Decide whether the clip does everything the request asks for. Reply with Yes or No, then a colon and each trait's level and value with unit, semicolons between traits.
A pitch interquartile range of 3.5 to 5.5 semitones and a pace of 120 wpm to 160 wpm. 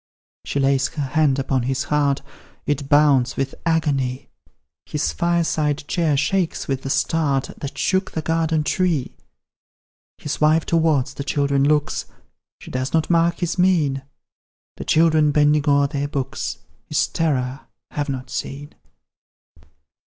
No: average, 2.8 semitones; slow, 135 wpm